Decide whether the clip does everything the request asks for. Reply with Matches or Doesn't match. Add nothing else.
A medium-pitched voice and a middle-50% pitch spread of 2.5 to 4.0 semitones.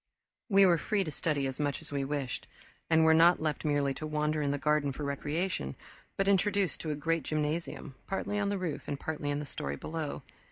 Matches